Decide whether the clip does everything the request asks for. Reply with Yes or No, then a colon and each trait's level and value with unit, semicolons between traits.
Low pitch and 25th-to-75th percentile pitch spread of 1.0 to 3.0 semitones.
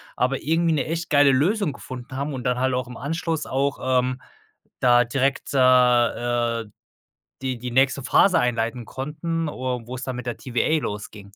Yes: low, 130 Hz; average, 2.7 semitones